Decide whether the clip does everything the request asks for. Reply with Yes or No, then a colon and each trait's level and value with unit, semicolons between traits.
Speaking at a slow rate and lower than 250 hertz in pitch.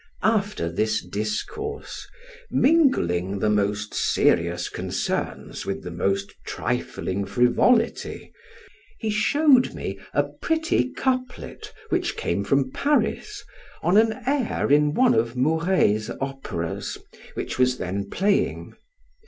Yes: slow, 110 wpm; low, 135 Hz